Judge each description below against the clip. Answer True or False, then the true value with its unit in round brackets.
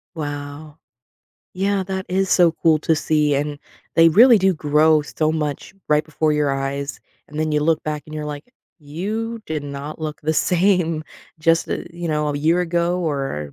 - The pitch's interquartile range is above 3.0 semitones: False (2.7 semitones)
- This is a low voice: False (155 Hz)